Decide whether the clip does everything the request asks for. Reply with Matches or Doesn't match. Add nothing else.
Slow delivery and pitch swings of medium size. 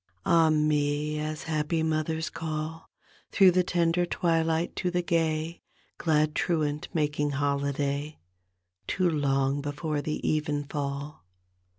Doesn't match